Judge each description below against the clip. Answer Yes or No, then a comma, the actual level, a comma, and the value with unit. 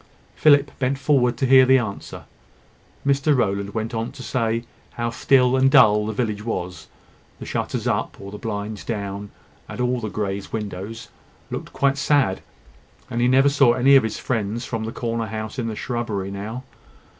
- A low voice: Yes, low, 115 Hz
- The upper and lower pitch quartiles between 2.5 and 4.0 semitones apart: Yes, average, 3.6 semitones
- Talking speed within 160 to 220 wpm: Yes, average, 180 wpm